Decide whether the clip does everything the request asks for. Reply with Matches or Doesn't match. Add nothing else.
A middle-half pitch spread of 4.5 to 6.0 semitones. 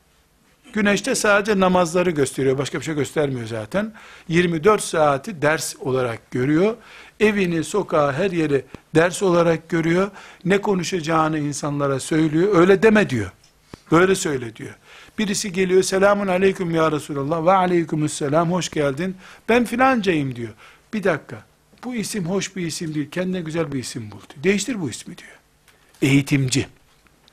Matches